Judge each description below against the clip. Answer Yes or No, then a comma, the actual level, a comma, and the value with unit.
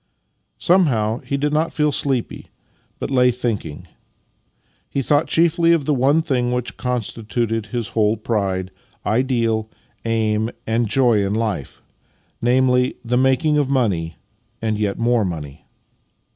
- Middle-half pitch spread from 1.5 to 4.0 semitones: Yes, average, 3.7 semitones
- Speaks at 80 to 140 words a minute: Yes, slow, 135 wpm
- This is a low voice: Yes, low, 120 Hz